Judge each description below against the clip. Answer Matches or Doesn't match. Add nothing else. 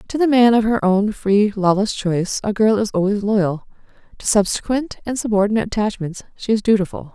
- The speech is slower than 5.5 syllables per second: Doesn't match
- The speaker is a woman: Matches